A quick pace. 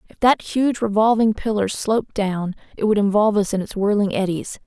No: average, 195 wpm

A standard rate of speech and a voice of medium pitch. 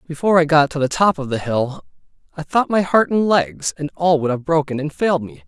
No: fast, 250 wpm; medium, 155 Hz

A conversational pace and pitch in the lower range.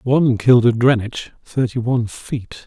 Yes: average, 160 wpm; low, 120 Hz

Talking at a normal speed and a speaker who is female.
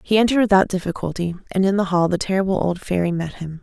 No: fast, 230 wpm; female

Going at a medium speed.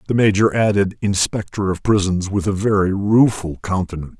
Yes: average, 155 wpm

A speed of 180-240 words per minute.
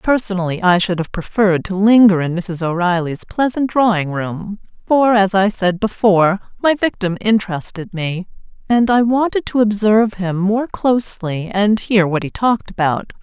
No: average, 165 wpm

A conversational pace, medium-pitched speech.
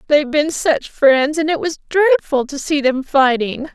No: average, 190 wpm; very high, 290 Hz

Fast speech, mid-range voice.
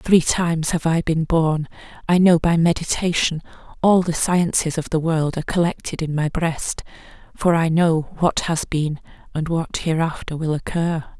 No: average, 170 wpm; medium, 165 Hz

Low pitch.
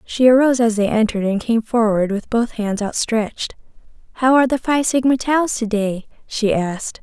No: high, 230 Hz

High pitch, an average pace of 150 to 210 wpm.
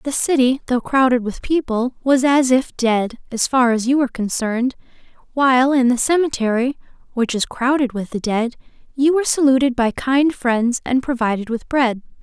Yes: very high, 255 Hz; average, 175 wpm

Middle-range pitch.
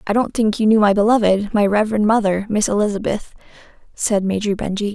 No: high, 210 Hz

